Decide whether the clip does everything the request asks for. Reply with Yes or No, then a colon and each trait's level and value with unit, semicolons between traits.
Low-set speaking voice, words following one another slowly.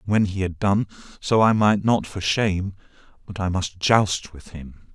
No: low, 100 Hz; fast, 205 wpm